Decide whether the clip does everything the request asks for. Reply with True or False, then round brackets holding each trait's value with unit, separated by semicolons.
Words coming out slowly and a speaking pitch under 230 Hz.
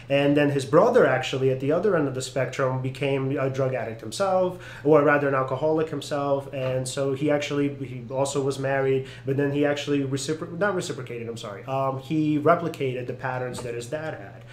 False (200 wpm; 135 Hz)